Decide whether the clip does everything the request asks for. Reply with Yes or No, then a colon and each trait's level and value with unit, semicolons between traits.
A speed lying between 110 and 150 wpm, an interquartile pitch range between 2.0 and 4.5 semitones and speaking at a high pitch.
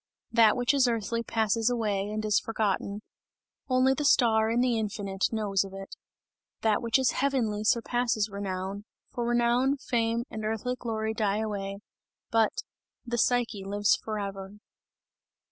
Yes: average, 145 wpm; average, 2.7 semitones; high, 220 Hz